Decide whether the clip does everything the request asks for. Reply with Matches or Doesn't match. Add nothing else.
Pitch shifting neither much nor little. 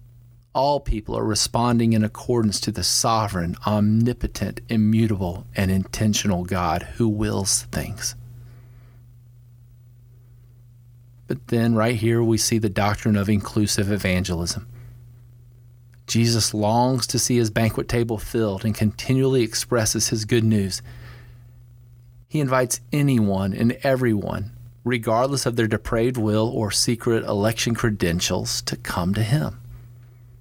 Doesn't match